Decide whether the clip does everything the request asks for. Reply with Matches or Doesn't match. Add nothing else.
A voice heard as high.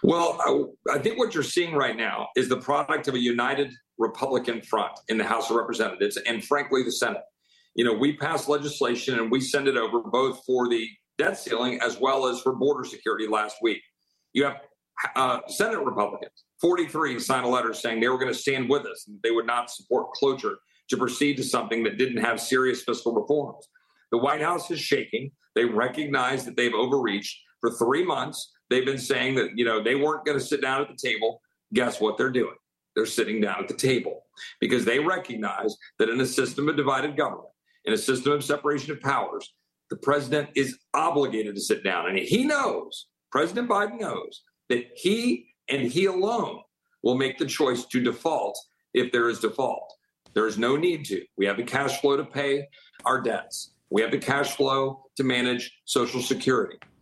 Doesn't match